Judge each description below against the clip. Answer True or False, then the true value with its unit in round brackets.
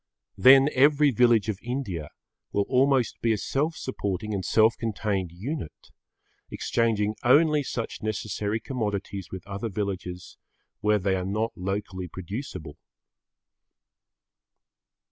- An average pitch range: True (4.4 semitones)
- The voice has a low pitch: True (105 Hz)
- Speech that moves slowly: True (115 wpm)